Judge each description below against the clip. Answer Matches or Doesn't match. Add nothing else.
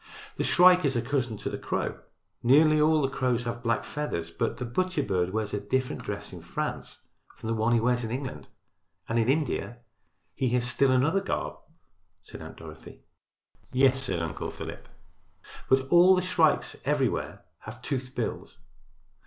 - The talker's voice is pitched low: Matches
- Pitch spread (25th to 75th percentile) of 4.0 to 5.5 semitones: Matches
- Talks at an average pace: Matches